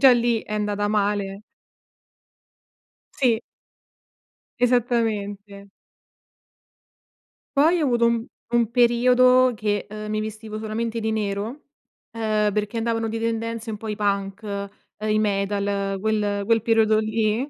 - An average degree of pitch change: No, narrow, 2.0 semitones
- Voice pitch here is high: Yes, high, 220 Hz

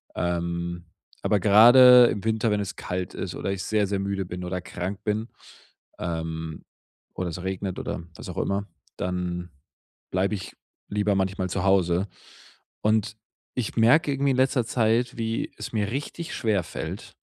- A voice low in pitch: Yes, low, 100 Hz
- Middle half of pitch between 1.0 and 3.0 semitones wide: No, average, 3.7 semitones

